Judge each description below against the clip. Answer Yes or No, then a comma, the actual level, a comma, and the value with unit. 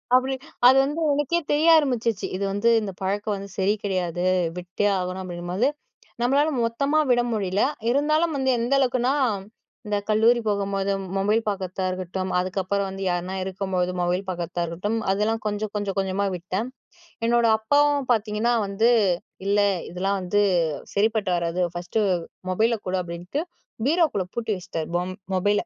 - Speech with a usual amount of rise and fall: Yes, average, 4.3 semitones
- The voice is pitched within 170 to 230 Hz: Yes, high, 205 Hz